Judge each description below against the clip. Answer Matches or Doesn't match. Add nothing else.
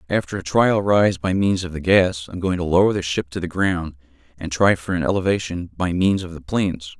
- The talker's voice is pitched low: Matches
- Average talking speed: Doesn't match